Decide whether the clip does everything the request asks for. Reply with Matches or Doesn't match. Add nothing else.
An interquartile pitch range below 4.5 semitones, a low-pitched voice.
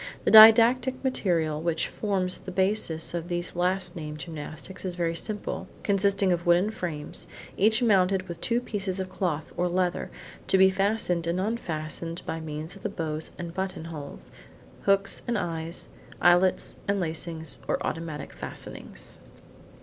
Doesn't match